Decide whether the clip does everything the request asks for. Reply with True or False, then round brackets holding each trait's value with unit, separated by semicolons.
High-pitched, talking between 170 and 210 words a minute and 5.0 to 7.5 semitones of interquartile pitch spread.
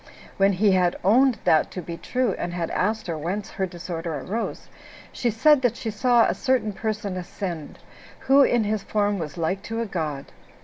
False (200 Hz; 190 wpm; 4.4 semitones)